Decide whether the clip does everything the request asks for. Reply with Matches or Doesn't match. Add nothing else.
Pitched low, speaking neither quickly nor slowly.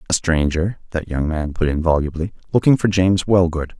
Matches